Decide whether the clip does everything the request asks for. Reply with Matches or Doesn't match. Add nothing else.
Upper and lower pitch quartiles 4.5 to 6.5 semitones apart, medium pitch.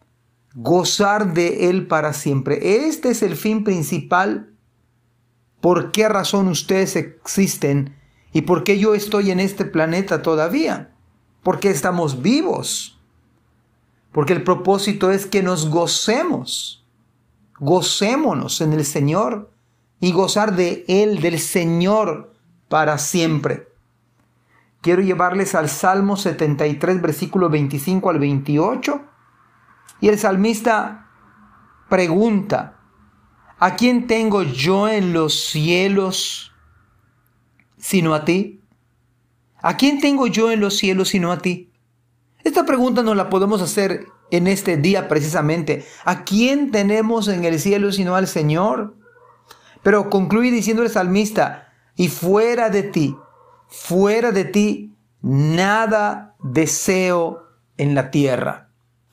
Matches